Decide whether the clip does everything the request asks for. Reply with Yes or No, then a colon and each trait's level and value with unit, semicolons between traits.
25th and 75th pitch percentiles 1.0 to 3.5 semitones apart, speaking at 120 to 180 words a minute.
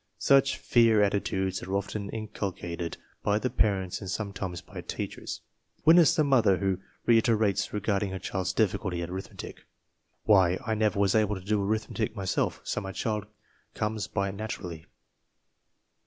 Yes: narrow, 2.4 semitones; average, 155 wpm